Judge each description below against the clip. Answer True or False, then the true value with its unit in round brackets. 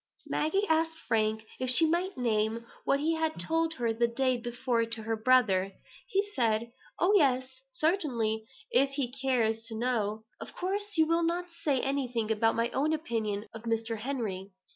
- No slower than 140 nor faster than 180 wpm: True (170 wpm)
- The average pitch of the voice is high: True (250 Hz)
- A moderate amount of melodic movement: False (5.9 semitones)